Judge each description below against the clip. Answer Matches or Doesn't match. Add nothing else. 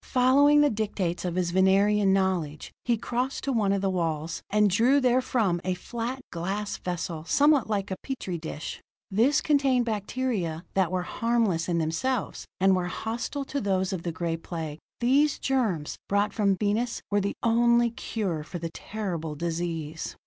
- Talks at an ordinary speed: Matches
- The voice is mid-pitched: Doesn't match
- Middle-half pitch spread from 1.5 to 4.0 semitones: Doesn't match